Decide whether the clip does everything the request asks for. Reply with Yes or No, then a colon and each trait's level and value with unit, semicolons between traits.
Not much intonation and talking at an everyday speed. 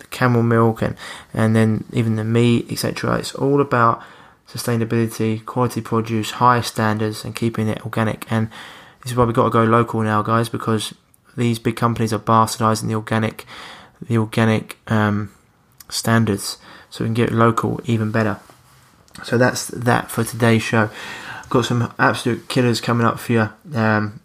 Yes: narrow, 1.3 semitones; average, 165 wpm